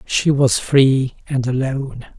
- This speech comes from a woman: No, male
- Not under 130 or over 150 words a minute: Yes, slow, 135 wpm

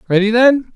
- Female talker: No, male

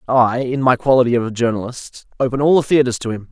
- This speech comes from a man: Yes, male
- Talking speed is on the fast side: Yes, fast, 215 wpm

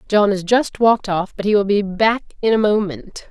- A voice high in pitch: Yes, high, 205 Hz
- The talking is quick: Yes, fast, 235 wpm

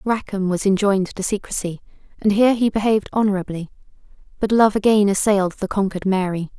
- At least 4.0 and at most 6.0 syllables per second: No, 6.3 syllables/s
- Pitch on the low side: No, high, 200 Hz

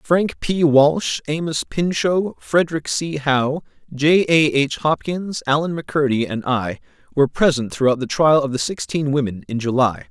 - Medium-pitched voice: Yes, medium, 150 Hz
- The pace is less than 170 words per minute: Yes, average, 160 wpm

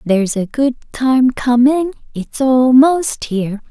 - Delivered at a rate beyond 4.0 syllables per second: No, 3.8 syllables/s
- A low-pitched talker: No, very high, 250 Hz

